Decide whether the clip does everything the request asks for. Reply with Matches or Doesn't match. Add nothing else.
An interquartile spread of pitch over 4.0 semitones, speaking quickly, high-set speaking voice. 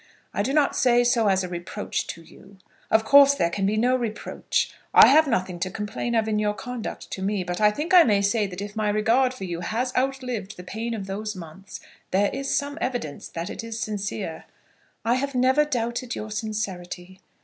Matches